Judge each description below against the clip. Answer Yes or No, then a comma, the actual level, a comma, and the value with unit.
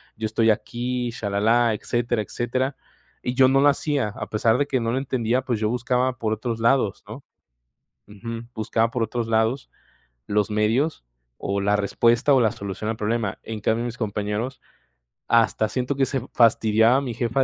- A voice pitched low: Yes, low, 115 Hz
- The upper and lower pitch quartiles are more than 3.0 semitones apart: No, narrow, 2.6 semitones